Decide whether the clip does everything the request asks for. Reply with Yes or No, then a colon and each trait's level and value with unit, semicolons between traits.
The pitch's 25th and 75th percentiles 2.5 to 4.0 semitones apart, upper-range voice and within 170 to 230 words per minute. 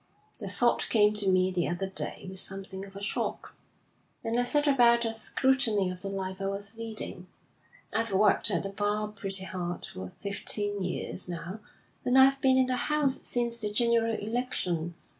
Yes: average, 3.7 semitones; high, 205 Hz; average, 180 wpm